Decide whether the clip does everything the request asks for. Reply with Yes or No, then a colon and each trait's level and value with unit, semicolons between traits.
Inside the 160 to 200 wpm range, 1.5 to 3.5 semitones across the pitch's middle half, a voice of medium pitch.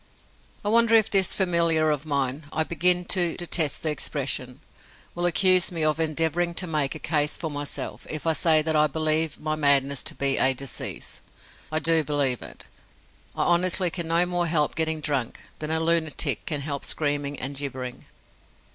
Yes: average, 180 wpm; average, 2.9 semitones; medium, 155 Hz